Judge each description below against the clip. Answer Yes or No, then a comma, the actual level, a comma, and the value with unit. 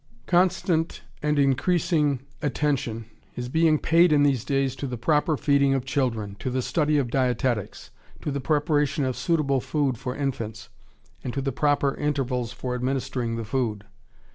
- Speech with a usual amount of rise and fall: Yes, average, 3.0 semitones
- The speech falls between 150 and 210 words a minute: Yes, average, 165 wpm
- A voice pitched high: No, low, 135 Hz